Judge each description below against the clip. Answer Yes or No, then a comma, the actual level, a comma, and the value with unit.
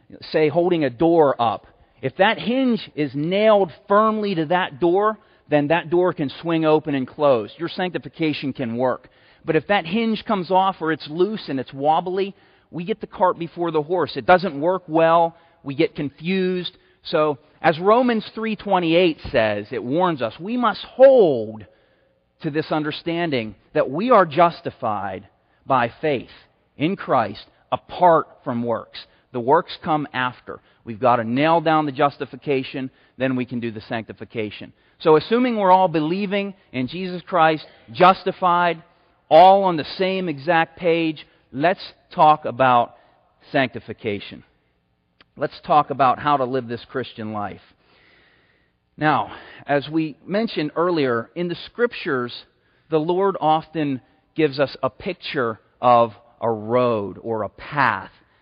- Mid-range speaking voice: Yes, medium, 160 Hz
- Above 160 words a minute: No, average, 145 wpm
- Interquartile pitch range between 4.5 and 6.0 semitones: Yes, wide, 5.6 semitones